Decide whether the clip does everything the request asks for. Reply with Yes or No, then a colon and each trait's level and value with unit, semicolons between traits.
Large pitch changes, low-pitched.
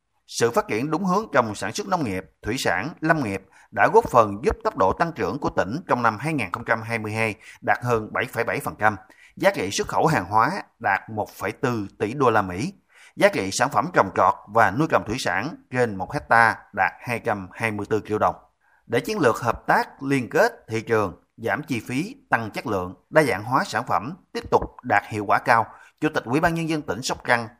Yes: wide, 6.0 semitones; low, 115 Hz